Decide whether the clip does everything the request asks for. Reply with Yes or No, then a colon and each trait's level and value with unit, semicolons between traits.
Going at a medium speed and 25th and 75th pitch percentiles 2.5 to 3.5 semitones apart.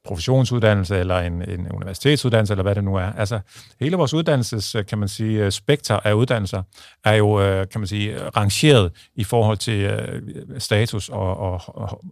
Yes: average, 160 wpm; average, 2.9 semitones